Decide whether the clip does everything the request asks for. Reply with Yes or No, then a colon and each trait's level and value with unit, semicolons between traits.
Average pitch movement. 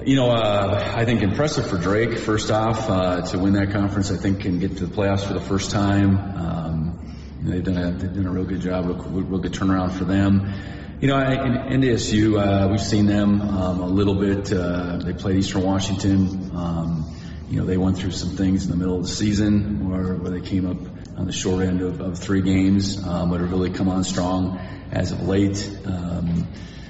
No: narrow, 1.7 semitones